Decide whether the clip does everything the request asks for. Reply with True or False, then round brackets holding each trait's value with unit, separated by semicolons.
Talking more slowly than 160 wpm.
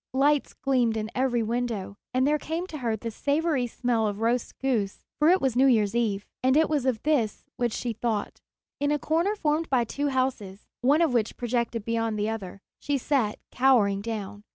False (200 wpm)